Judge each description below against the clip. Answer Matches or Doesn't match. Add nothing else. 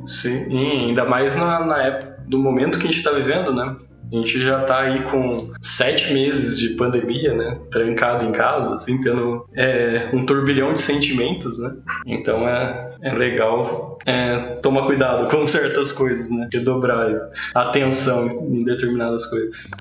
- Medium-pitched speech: Doesn't match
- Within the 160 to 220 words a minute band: Matches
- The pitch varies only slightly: Matches